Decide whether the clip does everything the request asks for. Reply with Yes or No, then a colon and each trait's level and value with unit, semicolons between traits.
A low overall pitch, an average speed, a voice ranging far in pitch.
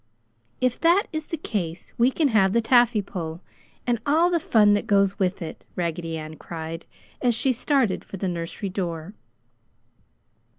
No: high, 205 Hz; average, 165 wpm; wide, 6.7 semitones